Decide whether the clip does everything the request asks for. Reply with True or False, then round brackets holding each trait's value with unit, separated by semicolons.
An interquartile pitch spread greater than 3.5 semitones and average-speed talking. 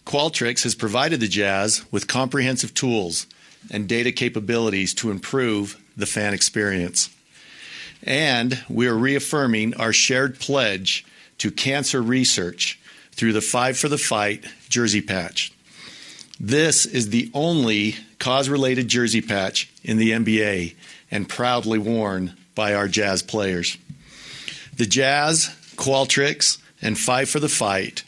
False (4.1 semitones; 130 wpm)